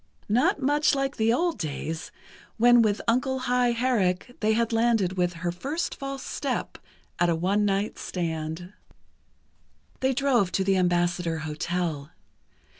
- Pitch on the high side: Yes, high, 205 Hz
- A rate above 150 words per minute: No, average, 140 wpm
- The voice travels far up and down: Yes, wide, 6.1 semitones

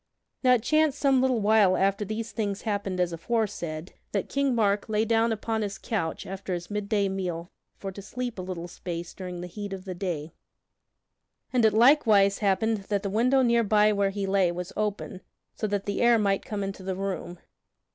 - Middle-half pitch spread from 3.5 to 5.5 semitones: No, average, 2.9 semitones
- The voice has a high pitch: Yes, high, 200 Hz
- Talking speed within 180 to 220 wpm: Yes, average, 195 wpm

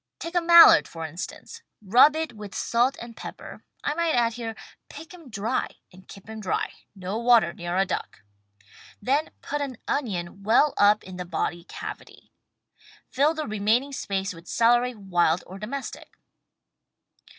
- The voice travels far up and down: Yes, wide, 6.5 semitones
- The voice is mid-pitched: No, high, 225 Hz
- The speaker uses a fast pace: No, average, 160 wpm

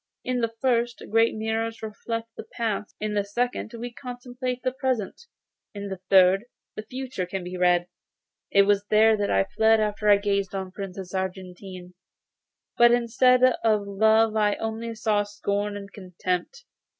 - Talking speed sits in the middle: Yes, average, 165 wpm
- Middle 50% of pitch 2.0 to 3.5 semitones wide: Yes, average, 2.8 semitones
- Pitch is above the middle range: Yes, high, 215 Hz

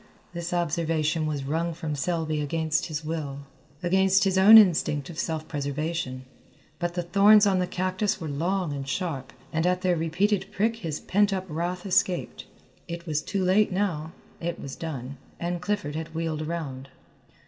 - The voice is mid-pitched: Yes, medium, 170 Hz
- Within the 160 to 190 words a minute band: Yes, average, 170 wpm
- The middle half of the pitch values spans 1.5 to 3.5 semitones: Yes, average, 3.2 semitones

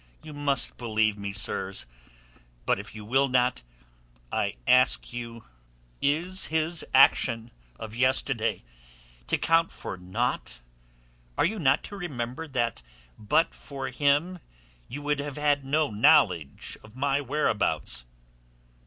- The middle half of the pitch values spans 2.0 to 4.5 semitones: No, average, 5.1 semitones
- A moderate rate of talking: No, slow, 125 wpm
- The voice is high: No, low, 130 Hz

